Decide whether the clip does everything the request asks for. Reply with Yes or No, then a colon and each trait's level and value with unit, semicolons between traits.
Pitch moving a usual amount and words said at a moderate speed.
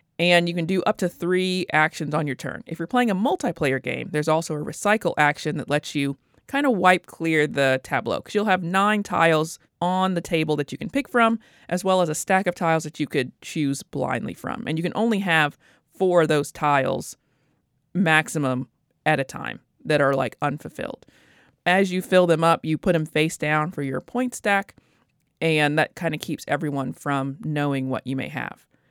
No: average, 3.8 semitones; fast, 210 wpm